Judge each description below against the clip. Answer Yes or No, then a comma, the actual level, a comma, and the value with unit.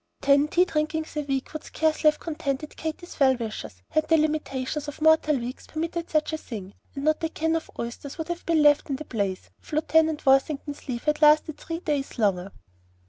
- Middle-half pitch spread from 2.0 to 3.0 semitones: Yes, average, 2.7 semitones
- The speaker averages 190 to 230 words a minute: Yes, average, 200 wpm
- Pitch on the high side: Yes, very high, 300 Hz